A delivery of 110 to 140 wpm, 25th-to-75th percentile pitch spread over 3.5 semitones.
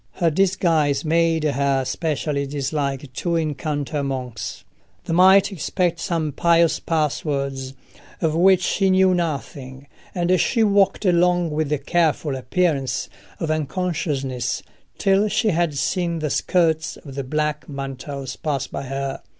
Yes: slow, 135 wpm; average, 4.0 semitones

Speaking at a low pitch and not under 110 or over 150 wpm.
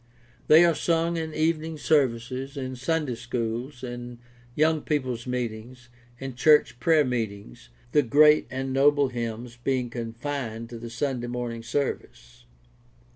Yes: low, 125 Hz; average, 140 wpm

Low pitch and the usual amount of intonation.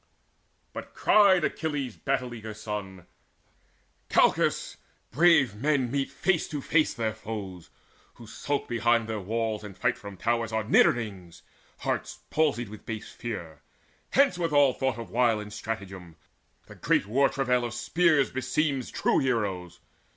Yes: low, 120 Hz; average, 4.7 semitones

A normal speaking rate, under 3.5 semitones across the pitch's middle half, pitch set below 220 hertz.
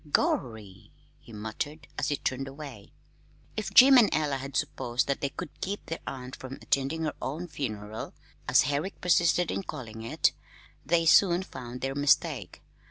No: average, 165 wpm; average, 4.5 semitones; medium, 140 Hz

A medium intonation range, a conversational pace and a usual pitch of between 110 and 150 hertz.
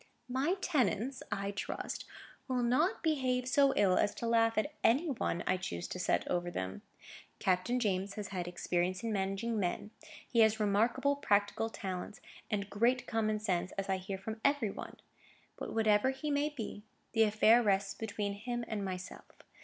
No: average, 3.9 semitones; average, 170 wpm; high, 215 Hz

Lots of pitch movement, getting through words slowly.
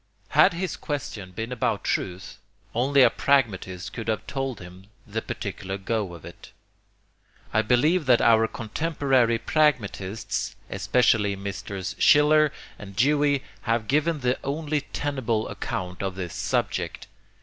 Yes: wide, 6.2 semitones; slow, 130 wpm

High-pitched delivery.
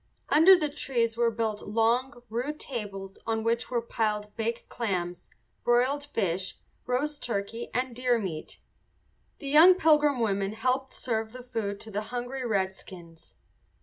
Yes: high, 230 Hz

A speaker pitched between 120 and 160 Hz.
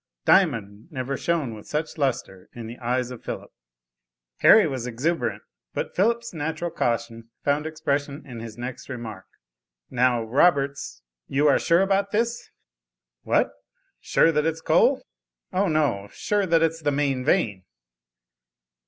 Yes: medium, 140 Hz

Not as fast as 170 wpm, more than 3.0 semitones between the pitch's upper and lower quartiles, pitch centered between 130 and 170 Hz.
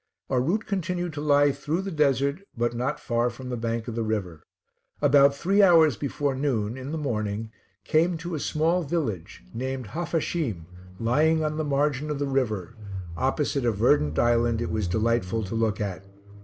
No: average, 180 wpm; average, 5.1 semitones; low, 135 Hz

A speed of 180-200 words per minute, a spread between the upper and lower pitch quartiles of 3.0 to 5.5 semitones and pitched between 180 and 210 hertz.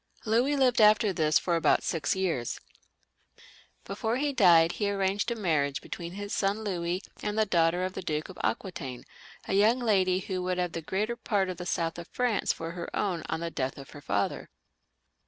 Yes: average, 195 wpm; average, 3.9 semitones; medium, 185 Hz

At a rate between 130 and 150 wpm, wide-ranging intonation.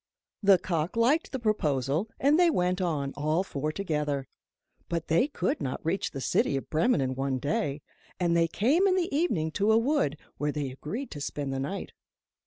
No: average, 195 wpm; wide, 7.2 semitones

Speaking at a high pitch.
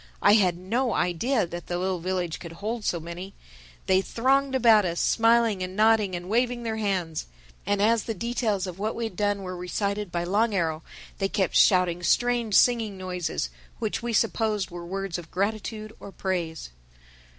Yes: high, 200 Hz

